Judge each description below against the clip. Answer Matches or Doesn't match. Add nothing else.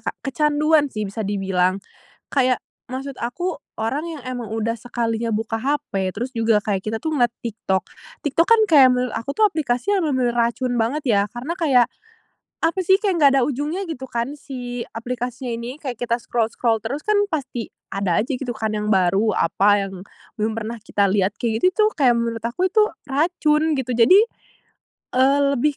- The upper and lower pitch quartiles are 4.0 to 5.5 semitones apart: Matches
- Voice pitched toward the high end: Matches